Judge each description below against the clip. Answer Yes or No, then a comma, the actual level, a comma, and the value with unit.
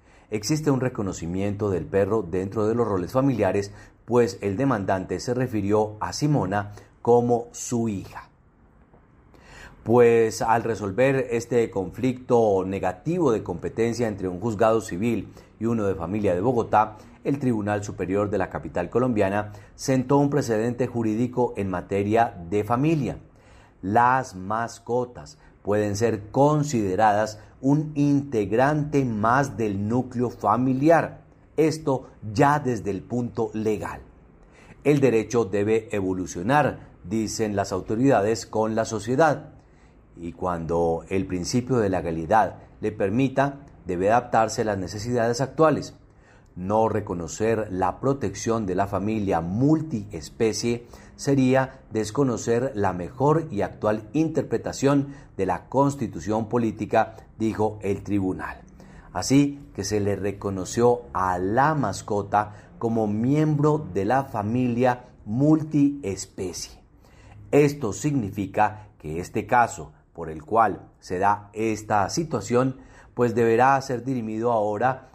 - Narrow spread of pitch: No, average, 4.3 semitones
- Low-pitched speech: Yes, low, 110 Hz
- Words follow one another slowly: Yes, slow, 115 wpm